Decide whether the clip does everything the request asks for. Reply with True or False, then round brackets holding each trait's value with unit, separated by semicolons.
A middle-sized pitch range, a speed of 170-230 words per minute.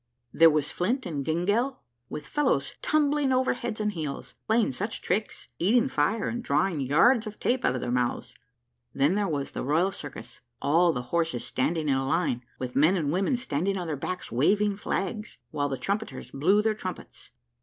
False (6.9 semitones; 185 wpm)